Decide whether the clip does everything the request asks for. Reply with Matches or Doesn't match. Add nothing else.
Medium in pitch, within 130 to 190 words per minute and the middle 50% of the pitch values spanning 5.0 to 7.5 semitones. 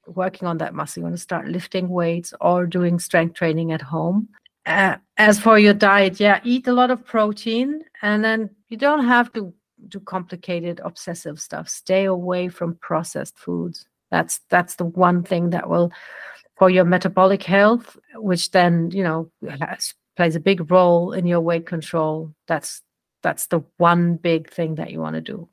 Doesn't match